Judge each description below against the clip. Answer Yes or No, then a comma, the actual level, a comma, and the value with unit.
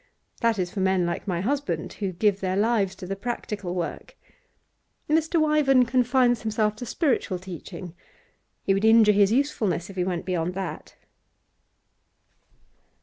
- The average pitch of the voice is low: No, high, 205 Hz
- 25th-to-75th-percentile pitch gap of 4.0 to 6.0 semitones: Yes, average, 4.7 semitones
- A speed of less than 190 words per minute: Yes, average, 145 wpm